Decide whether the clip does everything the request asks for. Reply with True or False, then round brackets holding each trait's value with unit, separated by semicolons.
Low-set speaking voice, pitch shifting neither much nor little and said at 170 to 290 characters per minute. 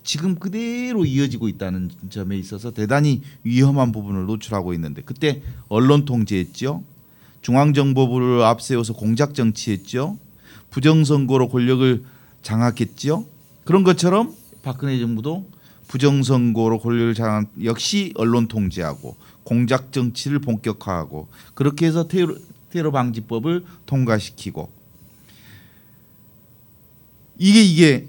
True (125 Hz; 4.8 semitones; 280 characters per minute)